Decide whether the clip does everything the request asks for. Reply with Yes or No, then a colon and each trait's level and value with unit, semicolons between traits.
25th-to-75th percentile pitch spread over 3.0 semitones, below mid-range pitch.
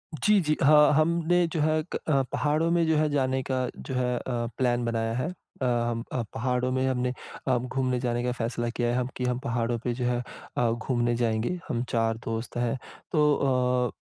No: average, 2.7 semitones; low, 125 Hz